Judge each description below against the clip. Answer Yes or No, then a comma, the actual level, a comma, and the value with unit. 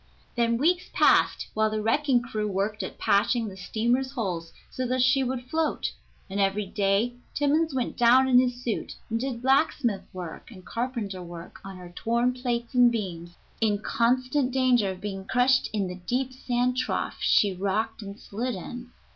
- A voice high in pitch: Yes, high, 235 Hz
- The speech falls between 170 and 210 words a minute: Yes, average, 175 wpm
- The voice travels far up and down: No, average, 4.2 semitones